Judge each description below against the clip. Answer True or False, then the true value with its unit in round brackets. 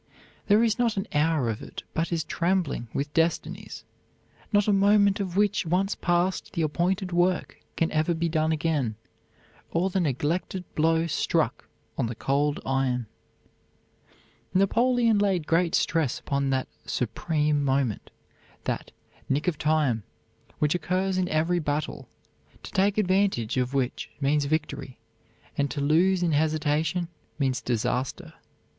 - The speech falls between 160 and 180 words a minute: False (140 wpm)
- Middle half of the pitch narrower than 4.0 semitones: False (4.6 semitones)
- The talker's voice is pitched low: False (160 Hz)